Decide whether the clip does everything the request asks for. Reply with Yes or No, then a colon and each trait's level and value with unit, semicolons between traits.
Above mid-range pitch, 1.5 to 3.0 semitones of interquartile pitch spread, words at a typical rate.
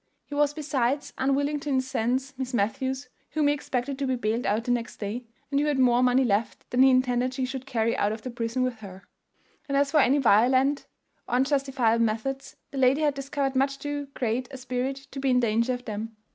No: very high, 255 Hz; narrow, 2.5 semitones; fast, 215 wpm